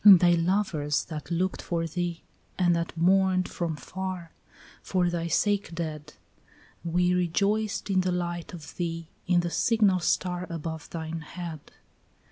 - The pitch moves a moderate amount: No, narrow, 1.9 semitones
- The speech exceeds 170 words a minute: No, average, 145 wpm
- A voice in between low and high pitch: Yes, medium, 175 Hz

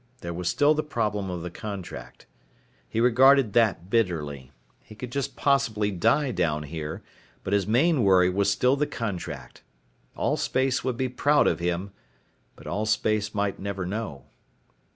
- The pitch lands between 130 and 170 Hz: No, low, 105 Hz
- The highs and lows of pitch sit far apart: Yes, wide, 5.9 semitones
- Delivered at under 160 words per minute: Yes, average, 150 wpm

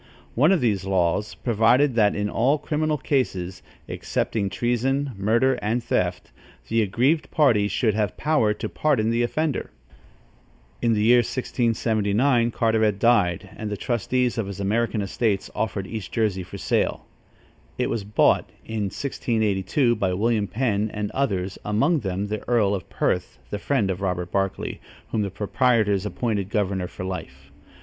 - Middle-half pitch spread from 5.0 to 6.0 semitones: No, average, 3.5 semitones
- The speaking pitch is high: No, low, 110 Hz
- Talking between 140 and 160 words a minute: Yes, average, 155 wpm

